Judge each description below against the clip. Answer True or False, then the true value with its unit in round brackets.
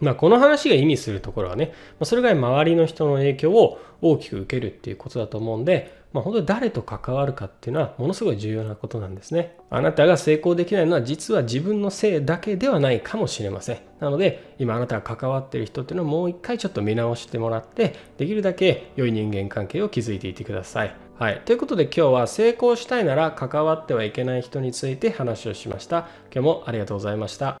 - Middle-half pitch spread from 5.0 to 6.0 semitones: False (7.2 semitones)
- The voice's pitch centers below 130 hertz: False (135 Hz)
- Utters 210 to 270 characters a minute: False (485 characters per minute)